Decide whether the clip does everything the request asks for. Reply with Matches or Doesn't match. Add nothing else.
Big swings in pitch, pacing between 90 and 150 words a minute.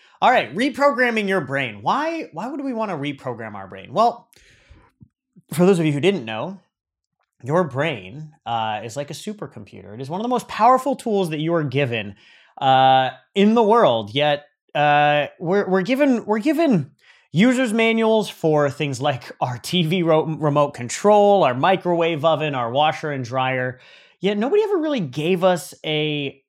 Doesn't match